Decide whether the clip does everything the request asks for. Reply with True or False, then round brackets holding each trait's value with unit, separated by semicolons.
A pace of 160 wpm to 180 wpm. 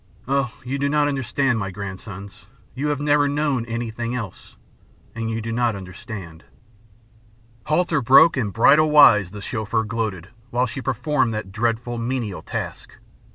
False (150 wpm)